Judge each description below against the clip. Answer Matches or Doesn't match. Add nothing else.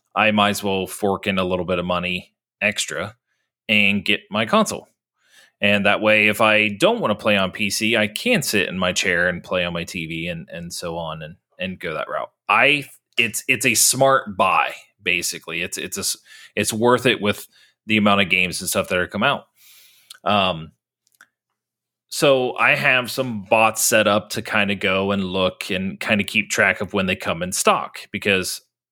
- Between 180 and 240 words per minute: Matches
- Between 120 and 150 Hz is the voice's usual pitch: Doesn't match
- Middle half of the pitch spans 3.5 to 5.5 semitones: Doesn't match